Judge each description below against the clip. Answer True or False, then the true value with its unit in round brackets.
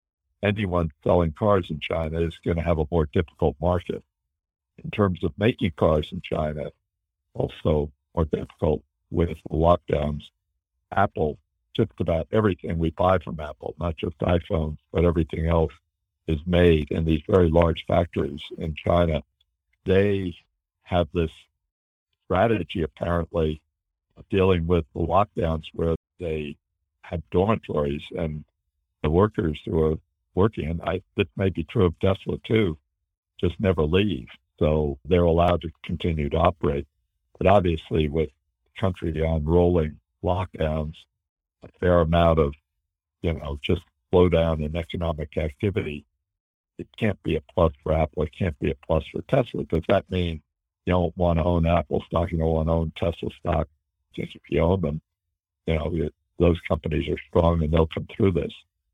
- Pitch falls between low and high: False (85 Hz)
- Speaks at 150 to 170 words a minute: True (155 wpm)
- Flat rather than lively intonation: True (2.2 semitones)